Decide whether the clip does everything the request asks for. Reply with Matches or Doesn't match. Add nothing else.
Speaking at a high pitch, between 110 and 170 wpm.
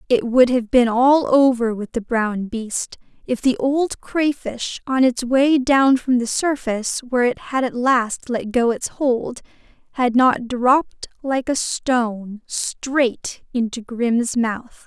Matches